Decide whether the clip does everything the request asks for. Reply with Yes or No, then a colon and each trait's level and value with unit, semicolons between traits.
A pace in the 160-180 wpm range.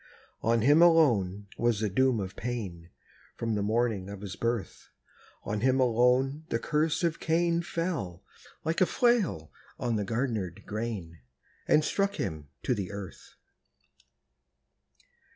No: slow, 135 wpm